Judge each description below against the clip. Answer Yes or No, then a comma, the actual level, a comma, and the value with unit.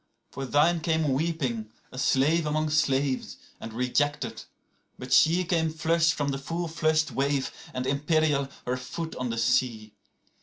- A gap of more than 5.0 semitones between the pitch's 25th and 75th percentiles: No, average, 3.6 semitones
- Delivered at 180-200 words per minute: No, average, 145 wpm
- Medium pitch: Yes, medium, 145 Hz